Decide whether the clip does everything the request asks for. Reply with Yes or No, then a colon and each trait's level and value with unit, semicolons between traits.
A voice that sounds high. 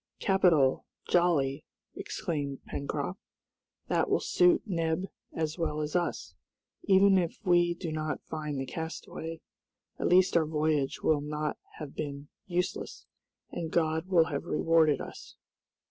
No: medium, 160 Hz